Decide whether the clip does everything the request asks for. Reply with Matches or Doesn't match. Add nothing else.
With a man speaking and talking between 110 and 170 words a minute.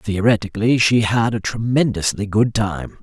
Matches